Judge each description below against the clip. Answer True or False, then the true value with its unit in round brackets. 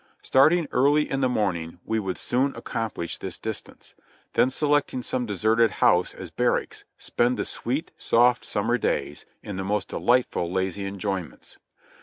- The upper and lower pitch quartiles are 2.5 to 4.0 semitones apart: False (4.7 semitones)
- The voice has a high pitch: False (115 Hz)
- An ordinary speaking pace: True (160 wpm)